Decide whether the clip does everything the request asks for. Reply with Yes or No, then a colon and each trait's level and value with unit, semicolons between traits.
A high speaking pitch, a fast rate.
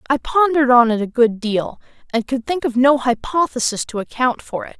Yes: very high, 255 Hz; fast, 215 wpm